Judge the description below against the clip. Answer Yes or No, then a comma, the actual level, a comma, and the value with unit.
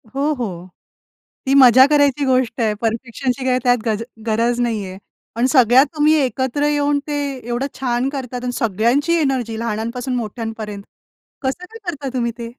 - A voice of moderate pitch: No, very high, 250 Hz